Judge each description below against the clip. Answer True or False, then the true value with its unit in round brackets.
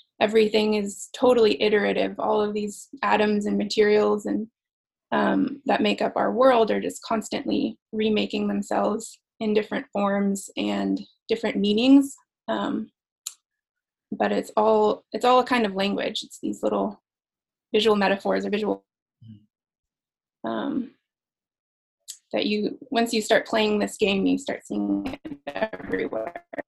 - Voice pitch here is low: False (215 Hz)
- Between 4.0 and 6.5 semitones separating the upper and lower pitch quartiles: False (2.8 semitones)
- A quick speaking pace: False (135 wpm)